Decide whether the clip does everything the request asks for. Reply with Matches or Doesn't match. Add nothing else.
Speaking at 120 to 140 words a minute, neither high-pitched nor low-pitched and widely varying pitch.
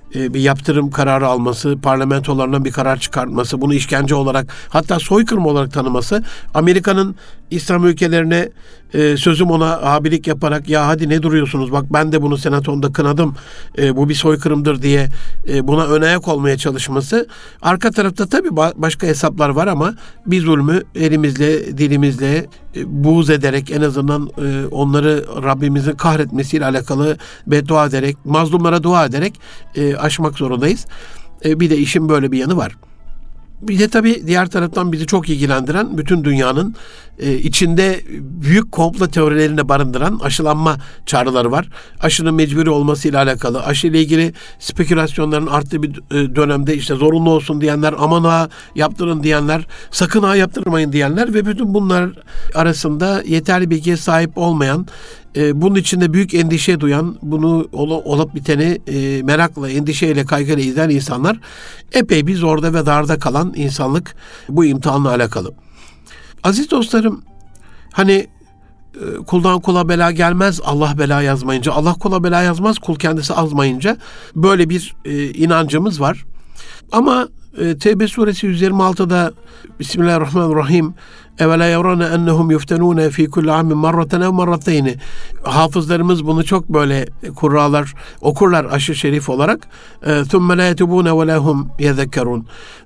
Doesn't match